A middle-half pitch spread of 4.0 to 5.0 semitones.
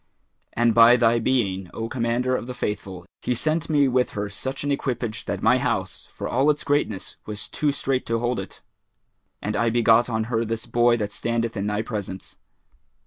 No: average, 2.8 semitones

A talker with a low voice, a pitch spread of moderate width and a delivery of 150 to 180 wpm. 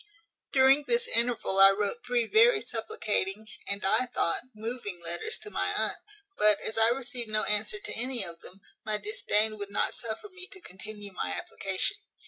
No: high, 220 Hz; average, 4.5 semitones; average, 175 wpm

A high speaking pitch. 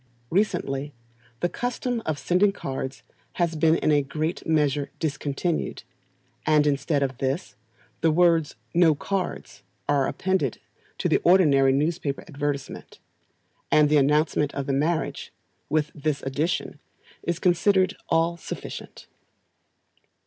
No: medium, 155 Hz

